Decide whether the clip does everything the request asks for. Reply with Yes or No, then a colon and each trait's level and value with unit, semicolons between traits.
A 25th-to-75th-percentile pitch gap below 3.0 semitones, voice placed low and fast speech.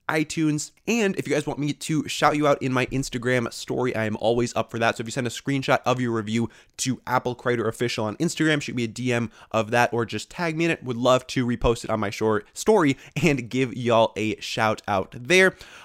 No: average, 4.0 semitones; low, 125 Hz; fast, 240 wpm